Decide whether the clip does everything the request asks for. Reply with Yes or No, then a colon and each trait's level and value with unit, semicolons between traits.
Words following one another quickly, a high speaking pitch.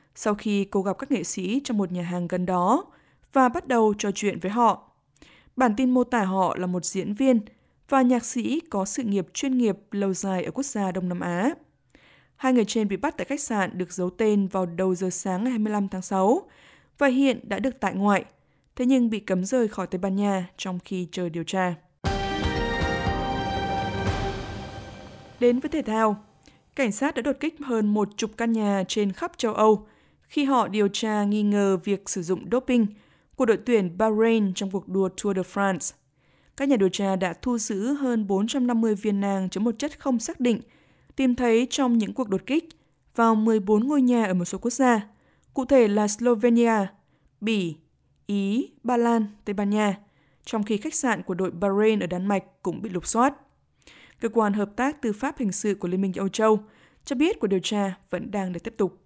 No: average, 205 wpm; high, 210 Hz